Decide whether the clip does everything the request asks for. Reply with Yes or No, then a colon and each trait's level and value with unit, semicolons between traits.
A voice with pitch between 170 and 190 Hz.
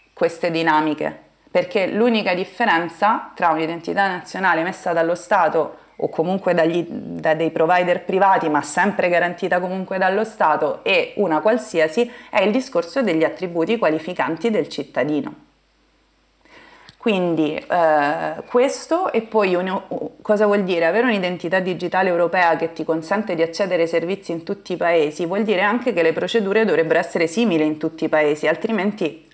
Yes: medium, 185 Hz